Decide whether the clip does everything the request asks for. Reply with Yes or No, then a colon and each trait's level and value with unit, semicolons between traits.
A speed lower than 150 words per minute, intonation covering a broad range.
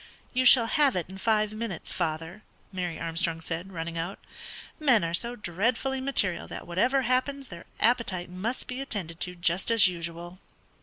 No: average, 165 wpm; wide, 6.0 semitones